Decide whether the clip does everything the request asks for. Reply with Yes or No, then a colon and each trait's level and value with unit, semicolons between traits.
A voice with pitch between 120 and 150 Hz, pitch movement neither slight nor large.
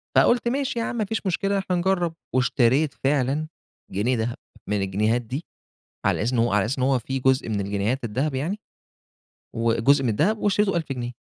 No: low, 135 Hz; wide, 7.2 semitones